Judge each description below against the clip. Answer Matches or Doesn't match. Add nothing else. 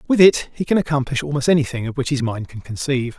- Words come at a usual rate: Doesn't match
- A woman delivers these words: Doesn't match